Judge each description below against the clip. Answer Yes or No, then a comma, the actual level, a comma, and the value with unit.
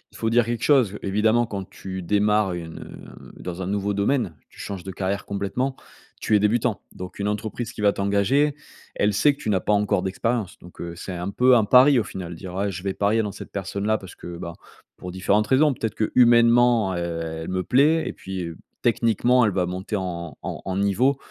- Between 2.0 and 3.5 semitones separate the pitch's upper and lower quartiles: No, average, 3.9 semitones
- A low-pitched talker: Yes, low, 100 Hz